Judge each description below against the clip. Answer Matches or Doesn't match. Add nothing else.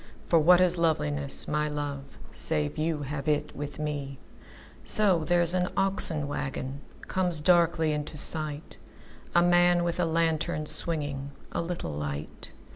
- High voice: Doesn't match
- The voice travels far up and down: Doesn't match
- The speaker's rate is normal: Doesn't match